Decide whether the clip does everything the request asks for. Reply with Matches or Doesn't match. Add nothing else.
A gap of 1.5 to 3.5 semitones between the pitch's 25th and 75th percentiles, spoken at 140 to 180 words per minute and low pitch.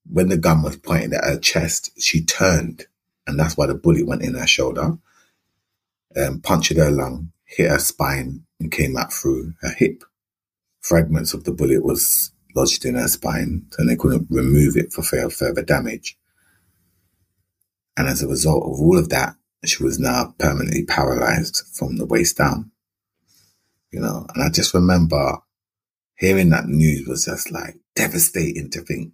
Doesn't match